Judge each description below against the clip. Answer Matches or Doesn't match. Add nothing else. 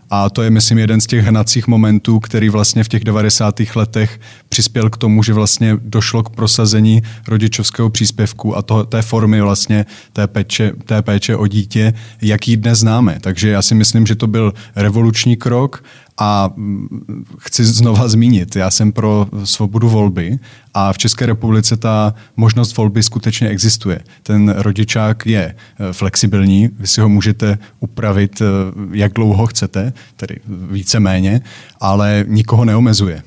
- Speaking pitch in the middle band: Doesn't match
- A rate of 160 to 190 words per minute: Doesn't match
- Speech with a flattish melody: Matches